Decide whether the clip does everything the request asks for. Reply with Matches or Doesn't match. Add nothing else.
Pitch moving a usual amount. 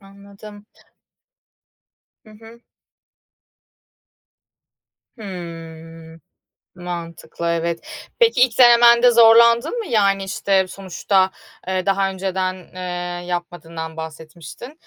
Matches